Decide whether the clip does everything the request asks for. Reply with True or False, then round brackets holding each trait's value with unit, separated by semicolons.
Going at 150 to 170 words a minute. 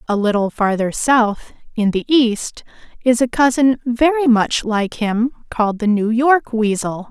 True (160 wpm)